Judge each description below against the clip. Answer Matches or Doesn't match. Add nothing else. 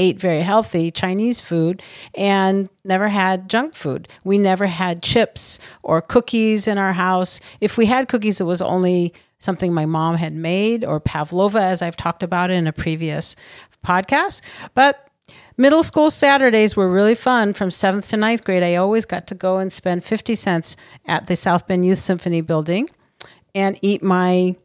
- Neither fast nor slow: Matches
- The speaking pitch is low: Doesn't match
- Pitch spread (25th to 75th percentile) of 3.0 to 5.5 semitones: Matches